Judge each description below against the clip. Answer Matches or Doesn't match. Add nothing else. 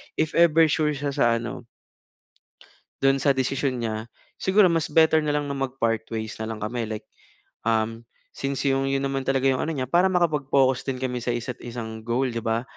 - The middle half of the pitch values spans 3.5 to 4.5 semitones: Matches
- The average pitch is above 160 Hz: Doesn't match